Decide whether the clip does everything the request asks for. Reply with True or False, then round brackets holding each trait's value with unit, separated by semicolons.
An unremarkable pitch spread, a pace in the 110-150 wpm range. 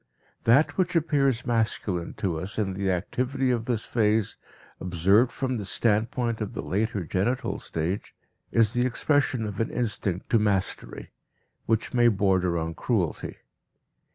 True (4.2 semitones; 145 wpm)